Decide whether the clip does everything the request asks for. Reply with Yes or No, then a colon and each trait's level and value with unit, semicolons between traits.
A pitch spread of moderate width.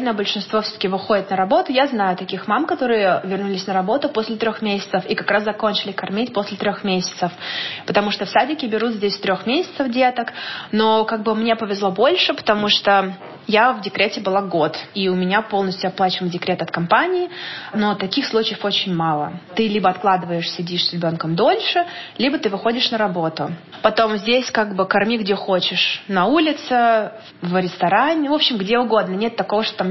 Yes: average, 3.1 semitones